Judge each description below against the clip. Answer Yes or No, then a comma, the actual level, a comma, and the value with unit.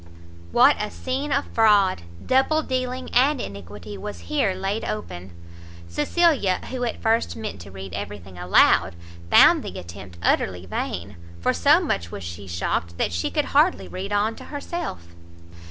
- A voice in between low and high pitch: No, low, 105 Hz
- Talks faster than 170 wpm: No, average, 160 wpm